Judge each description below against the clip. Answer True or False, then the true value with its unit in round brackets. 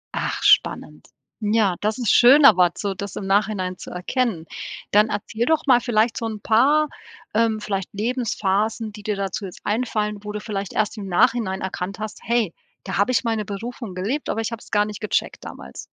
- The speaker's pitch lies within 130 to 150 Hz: False (215 Hz)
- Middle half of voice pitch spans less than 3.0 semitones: True (2.6 semitones)